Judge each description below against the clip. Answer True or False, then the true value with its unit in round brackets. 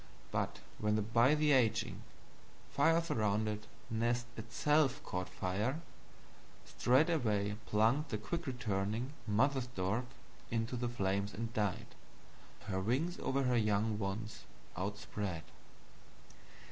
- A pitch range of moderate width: True (4.0 semitones)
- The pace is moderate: False (95 wpm)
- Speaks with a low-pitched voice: True (115 Hz)